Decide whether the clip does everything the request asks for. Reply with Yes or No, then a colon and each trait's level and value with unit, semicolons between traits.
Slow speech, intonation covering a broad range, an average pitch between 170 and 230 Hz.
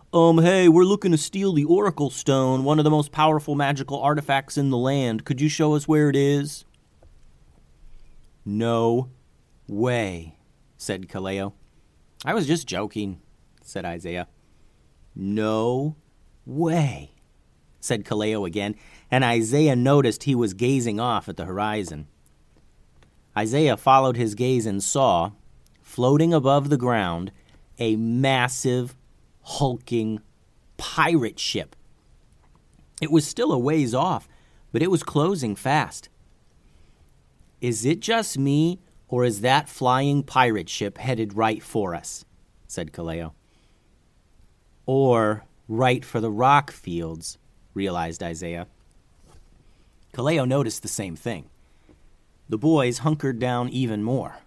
No: slow, 125 wpm; wide, 8.1 semitones; low, 120 Hz